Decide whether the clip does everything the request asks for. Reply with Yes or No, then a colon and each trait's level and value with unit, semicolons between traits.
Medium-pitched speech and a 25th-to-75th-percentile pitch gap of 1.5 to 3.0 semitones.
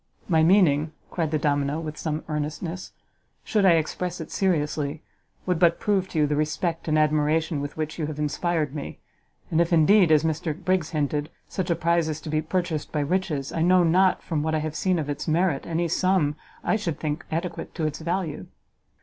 Yes: medium, 160 Hz; narrow, 2.5 semitones